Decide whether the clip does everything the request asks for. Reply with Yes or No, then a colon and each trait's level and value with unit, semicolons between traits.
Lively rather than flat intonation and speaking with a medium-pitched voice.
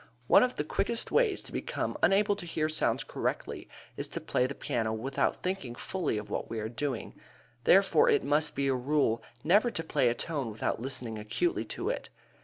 Yes: wide, 8.4 semitones; medium, 145 Hz